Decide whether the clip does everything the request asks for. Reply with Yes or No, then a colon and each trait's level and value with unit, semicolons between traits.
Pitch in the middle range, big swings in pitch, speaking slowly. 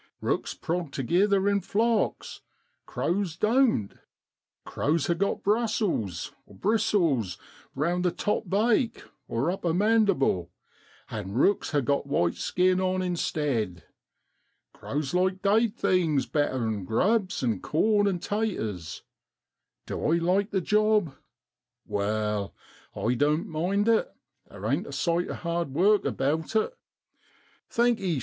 Yes: medium, 175 Hz; wide, 6.8 semitones; slow, 120 wpm